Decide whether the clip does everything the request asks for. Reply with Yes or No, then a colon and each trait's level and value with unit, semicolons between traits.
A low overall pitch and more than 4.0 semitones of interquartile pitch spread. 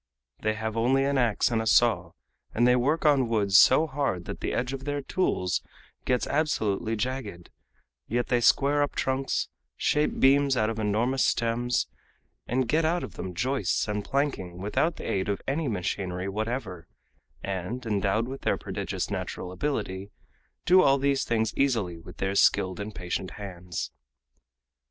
Yes: low, 115 Hz; average, 5.3 semitones